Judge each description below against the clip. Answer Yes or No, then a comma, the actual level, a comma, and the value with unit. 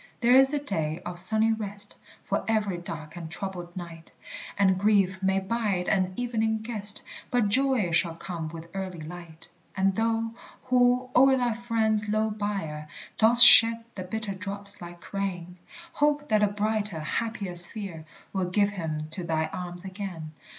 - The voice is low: No, high, 200 Hz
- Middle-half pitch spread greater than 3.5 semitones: Yes, average, 4.0 semitones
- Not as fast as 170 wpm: Yes, average, 160 wpm